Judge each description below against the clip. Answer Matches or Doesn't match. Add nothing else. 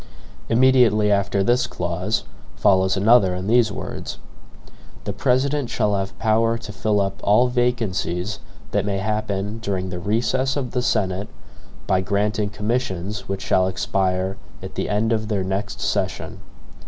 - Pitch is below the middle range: Matches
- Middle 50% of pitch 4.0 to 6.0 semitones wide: Doesn't match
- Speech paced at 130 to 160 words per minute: Matches